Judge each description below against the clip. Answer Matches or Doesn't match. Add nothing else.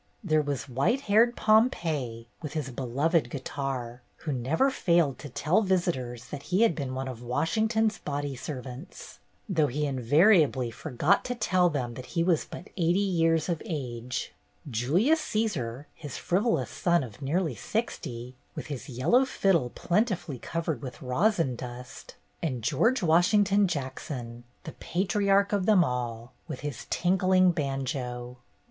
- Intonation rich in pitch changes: Matches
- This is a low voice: Doesn't match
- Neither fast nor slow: Matches